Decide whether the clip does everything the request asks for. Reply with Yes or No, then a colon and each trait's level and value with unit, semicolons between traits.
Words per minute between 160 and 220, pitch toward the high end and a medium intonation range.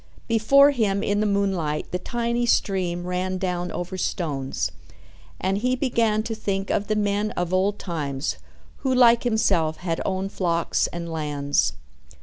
No: average, 150 wpm; high, 195 Hz; average, 3.9 semitones